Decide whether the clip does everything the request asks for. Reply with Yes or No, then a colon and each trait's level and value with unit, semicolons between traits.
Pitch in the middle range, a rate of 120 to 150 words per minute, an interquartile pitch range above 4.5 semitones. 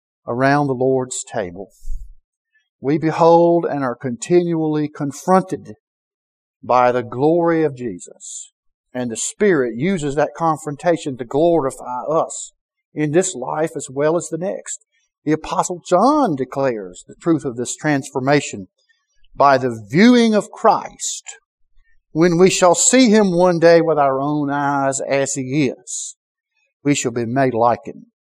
Yes: medium, 155 Hz; average, 140 wpm; average, 5.2 semitones